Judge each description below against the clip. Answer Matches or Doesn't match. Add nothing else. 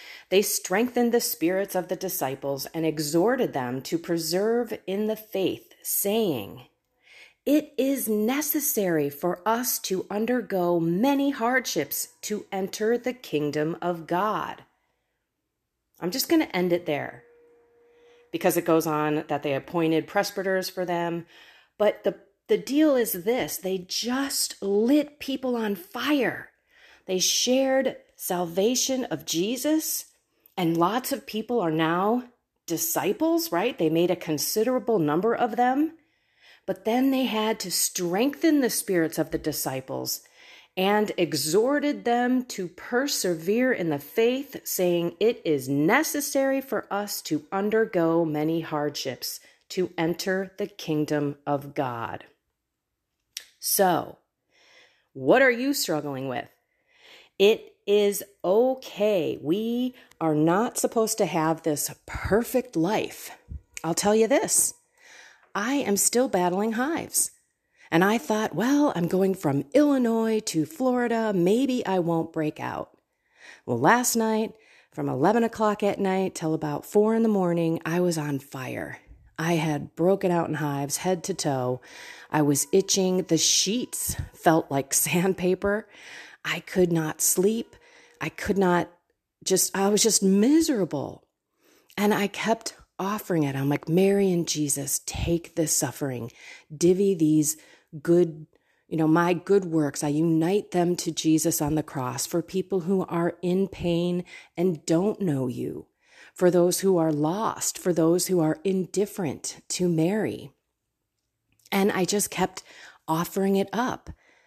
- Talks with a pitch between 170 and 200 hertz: Matches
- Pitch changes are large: Matches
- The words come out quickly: Doesn't match